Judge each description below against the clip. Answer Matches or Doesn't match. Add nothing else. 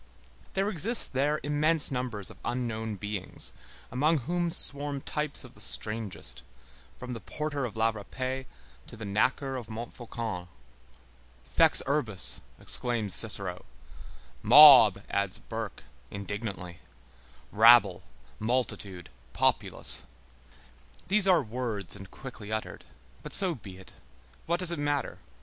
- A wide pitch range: Matches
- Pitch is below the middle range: Matches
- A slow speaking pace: Matches